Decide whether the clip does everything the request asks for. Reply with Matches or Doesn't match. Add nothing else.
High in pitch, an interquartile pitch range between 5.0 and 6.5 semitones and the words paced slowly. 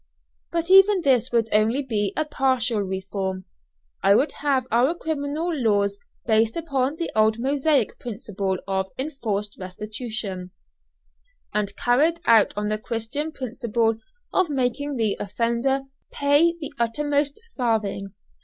Matches